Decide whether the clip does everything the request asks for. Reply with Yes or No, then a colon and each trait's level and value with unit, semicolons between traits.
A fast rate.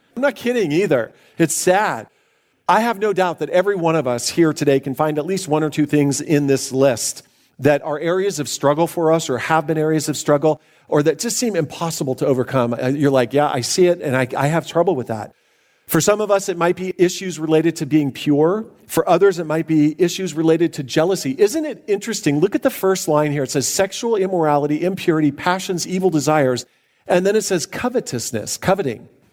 Yes: fast, 215 wpm